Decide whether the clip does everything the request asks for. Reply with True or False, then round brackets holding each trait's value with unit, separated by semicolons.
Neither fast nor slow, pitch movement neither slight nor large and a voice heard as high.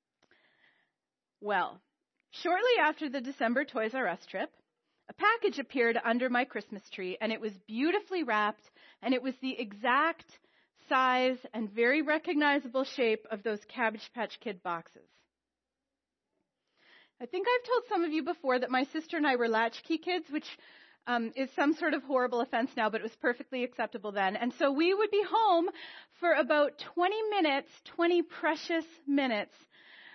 False (160 wpm; 5.8 semitones; 265 Hz)